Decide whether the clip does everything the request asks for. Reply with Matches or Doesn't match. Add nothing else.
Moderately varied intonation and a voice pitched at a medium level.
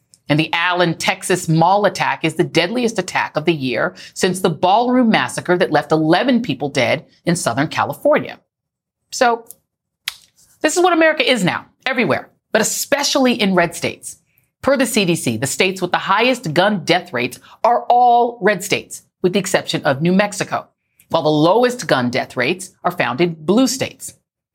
Doesn't match